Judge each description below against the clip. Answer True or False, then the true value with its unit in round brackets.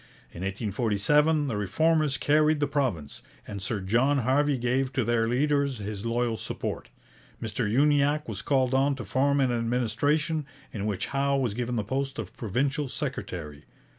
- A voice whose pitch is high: False (130 Hz)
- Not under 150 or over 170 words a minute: True (160 wpm)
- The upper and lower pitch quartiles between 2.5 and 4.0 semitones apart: False (4.6 semitones)